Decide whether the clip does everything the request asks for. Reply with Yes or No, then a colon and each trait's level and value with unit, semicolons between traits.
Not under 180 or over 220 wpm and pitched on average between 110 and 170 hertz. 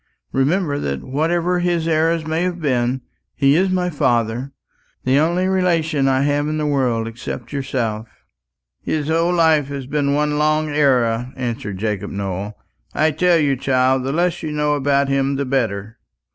No: average, 165 wpm; medium, 140 Hz